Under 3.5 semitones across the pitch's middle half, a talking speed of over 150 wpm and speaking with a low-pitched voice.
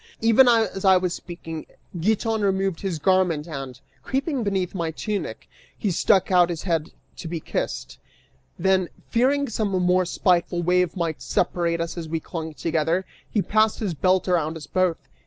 No: average, 3.1 semitones; average, 165 wpm; medium, 180 Hz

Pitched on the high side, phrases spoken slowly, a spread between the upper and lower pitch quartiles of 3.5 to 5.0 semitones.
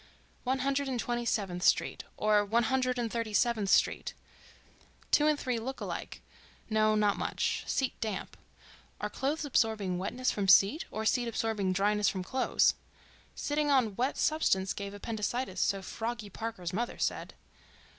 No: high, 225 Hz; average, 145 wpm; average, 3.9 semitones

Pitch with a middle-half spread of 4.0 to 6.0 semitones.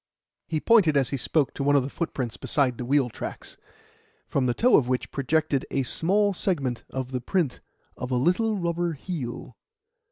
Yes: average, 5.1 semitones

